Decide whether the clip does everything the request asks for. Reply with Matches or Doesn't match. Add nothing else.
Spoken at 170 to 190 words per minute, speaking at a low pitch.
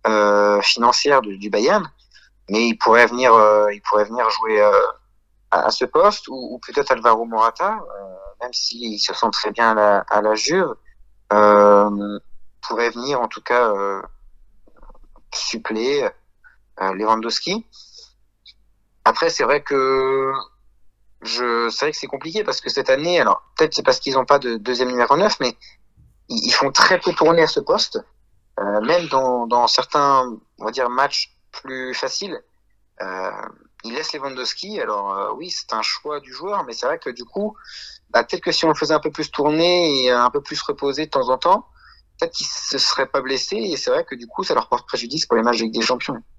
Doesn't match